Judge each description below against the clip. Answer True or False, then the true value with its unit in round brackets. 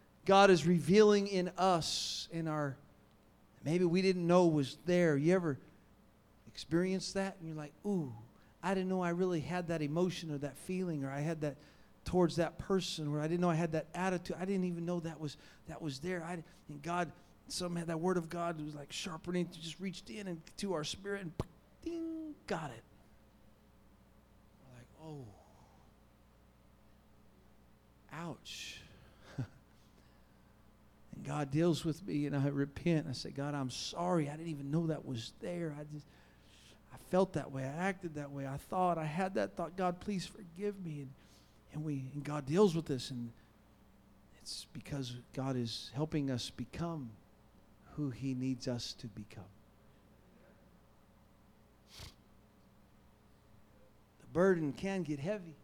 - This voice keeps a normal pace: True (160 wpm)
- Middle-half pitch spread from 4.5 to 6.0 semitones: True (5.2 semitones)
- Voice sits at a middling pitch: True (155 Hz)